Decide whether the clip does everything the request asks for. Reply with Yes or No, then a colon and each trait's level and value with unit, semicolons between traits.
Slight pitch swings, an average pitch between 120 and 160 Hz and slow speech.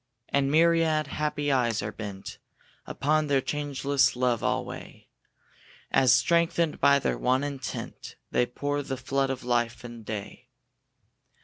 No: average, 3.1 semitones; low, 135 Hz; slow, 130 wpm